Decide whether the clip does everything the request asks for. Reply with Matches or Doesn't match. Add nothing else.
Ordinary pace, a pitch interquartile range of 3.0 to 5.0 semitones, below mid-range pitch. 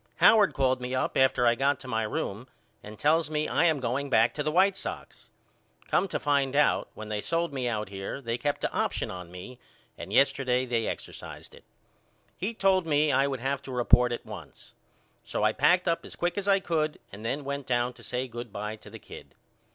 Doesn't match